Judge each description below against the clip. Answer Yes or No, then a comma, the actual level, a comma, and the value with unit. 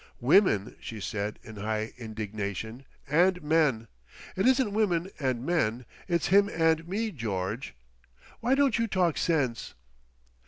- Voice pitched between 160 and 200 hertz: No, medium, 150 Hz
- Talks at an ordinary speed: No, slow, 125 wpm